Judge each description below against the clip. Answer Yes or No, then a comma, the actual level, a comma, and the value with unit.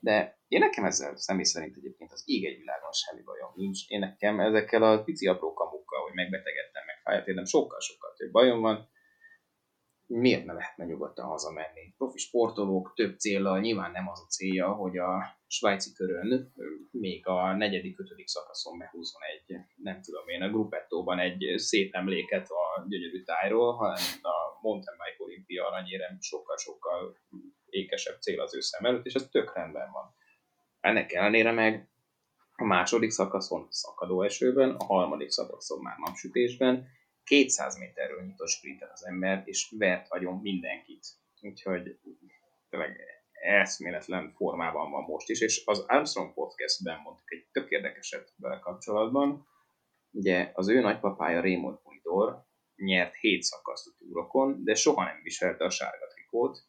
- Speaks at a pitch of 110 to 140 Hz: Yes, low, 115 Hz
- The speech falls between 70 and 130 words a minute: No, average, 145 wpm